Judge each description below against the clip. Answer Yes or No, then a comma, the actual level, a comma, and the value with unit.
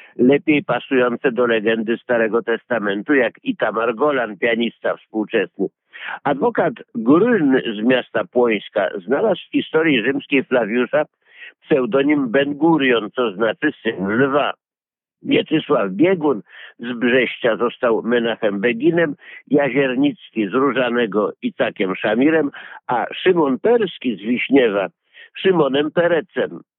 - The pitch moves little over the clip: No, average, 4.7 semitones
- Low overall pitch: Yes, low, 130 Hz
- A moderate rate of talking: No, slow, 105 wpm